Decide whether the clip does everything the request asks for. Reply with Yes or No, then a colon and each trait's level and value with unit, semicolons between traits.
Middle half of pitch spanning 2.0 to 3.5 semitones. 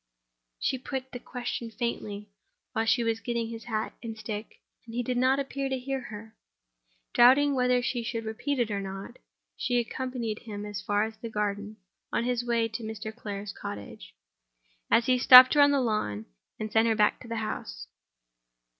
Yes: average, 2.8 semitones